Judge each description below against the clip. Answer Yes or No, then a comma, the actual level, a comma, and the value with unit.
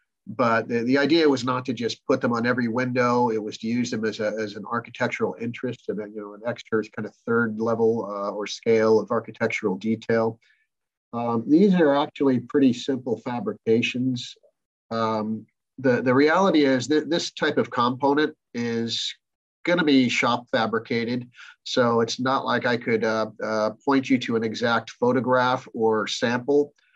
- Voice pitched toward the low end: Yes, low, 120 Hz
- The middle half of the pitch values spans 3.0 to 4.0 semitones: No, narrow, 2.4 semitones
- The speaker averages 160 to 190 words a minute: Yes, average, 175 wpm